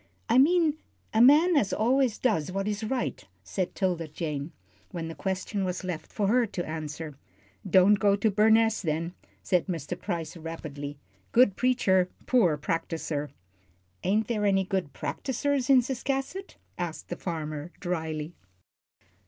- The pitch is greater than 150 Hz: Yes, high, 190 Hz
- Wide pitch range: Yes, wide, 5.9 semitones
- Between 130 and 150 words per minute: Yes, average, 145 wpm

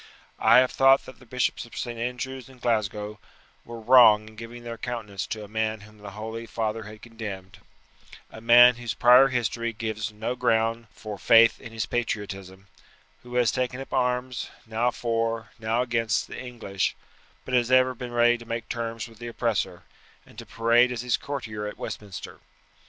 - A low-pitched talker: Yes, low, 115 Hz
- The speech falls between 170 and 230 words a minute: Yes, average, 180 wpm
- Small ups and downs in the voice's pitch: Yes, narrow, 2.1 semitones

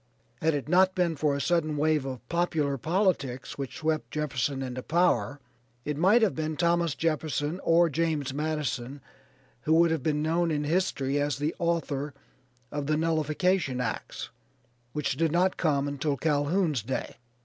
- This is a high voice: No, medium, 155 Hz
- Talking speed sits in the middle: Yes, average, 160 wpm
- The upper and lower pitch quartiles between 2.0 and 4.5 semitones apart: Yes, average, 3.0 semitones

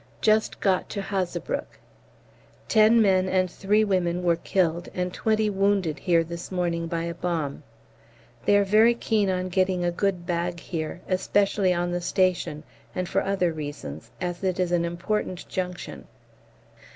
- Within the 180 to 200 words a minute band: No, average, 155 wpm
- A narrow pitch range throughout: Yes, narrow, 2.3 semitones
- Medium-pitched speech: Yes, medium, 180 Hz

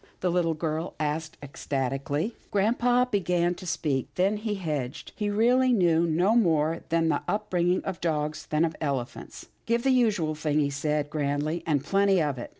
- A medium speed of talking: Yes, average, 185 wpm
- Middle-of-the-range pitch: Yes, medium, 165 Hz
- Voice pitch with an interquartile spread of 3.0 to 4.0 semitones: No, average, 4.7 semitones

